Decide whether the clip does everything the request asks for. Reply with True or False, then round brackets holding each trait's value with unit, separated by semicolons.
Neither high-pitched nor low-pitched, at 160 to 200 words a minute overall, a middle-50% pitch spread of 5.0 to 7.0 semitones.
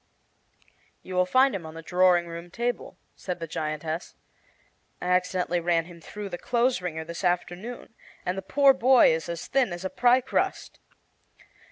True (180 Hz; 170 wpm; 5.6 semitones)